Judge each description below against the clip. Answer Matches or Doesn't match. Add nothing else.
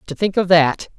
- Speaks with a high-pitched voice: Doesn't match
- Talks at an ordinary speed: Doesn't match